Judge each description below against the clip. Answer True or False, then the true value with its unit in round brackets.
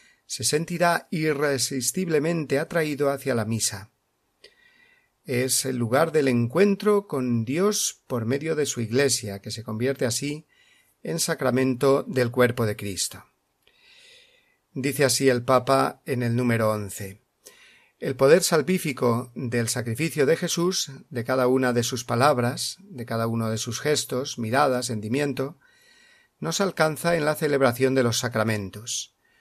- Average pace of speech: True (135 wpm)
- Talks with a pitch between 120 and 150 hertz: True (135 Hz)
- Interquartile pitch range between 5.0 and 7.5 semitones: True (5.3 semitones)